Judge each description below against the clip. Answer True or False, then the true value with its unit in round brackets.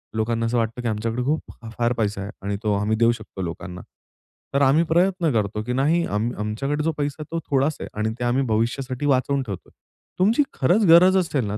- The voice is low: True (125 Hz)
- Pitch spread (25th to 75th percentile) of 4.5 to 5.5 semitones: True (5.2 semitones)